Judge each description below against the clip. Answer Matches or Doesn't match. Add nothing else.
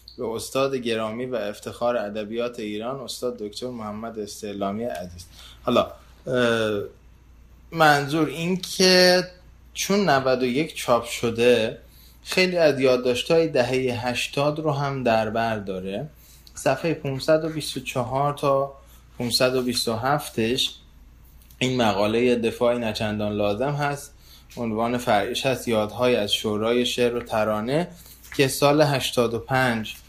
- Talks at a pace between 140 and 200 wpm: Doesn't match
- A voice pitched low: Matches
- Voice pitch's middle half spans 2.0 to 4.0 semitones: Doesn't match